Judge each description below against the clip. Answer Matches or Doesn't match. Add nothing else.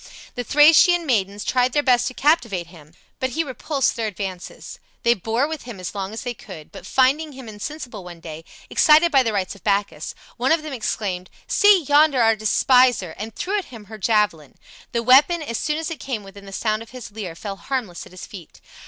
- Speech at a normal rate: Doesn't match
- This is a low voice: Doesn't match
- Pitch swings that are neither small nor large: Doesn't match